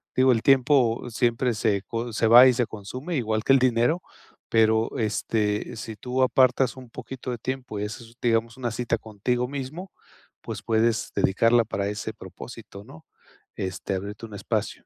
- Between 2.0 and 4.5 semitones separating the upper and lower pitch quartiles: Yes, average, 2.8 semitones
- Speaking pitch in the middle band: No, low, 115 Hz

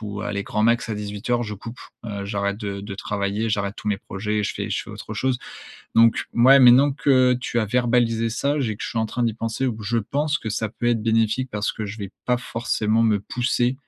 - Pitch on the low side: Yes, low, 115 Hz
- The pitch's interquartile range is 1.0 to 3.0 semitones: Yes, average, 2.7 semitones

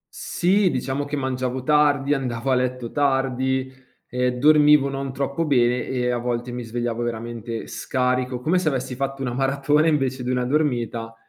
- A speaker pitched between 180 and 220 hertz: No, low, 130 Hz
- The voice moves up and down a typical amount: No, narrow, 2.1 semitones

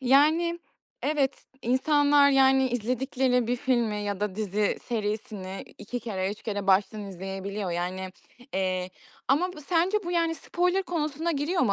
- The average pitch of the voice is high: Yes, high, 245 Hz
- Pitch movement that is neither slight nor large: No, wide, 6.5 semitones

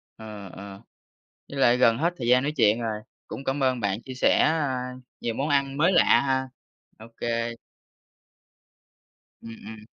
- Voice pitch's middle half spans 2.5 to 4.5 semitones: Yes, average, 3.7 semitones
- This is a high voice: No, low, 125 Hz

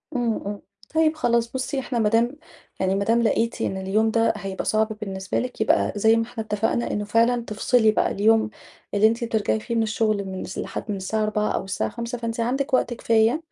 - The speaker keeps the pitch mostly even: Yes, narrow, 2.1 semitones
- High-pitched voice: Yes, high, 225 Hz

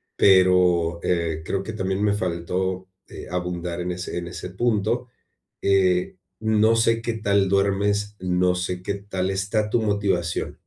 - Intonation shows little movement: Yes, narrow, 2.3 semitones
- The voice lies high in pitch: No, very low, 95 Hz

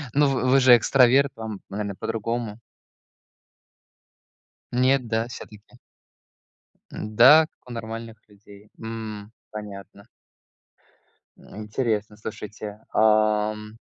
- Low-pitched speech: Yes, low, 110 Hz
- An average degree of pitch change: No, narrow, 2.2 semitones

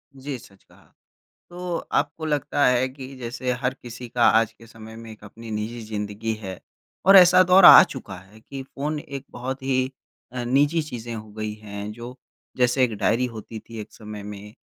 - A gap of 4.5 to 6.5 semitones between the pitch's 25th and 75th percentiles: No, average, 3.8 semitones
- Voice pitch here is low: Yes, low, 120 Hz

